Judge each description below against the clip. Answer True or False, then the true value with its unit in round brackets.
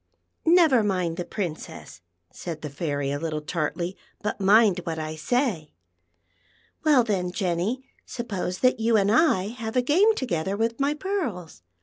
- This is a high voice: True (200 Hz)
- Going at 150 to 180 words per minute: True (155 wpm)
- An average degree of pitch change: False (6.7 semitones)